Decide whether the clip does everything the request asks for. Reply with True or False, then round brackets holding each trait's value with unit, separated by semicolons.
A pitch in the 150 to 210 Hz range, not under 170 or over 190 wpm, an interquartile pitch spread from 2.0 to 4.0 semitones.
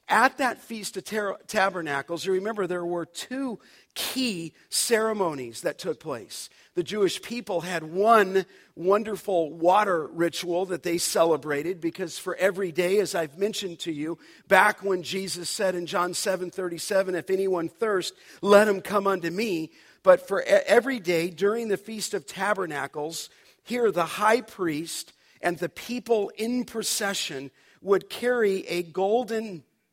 False (190 Hz; 150 wpm; 3.4 semitones)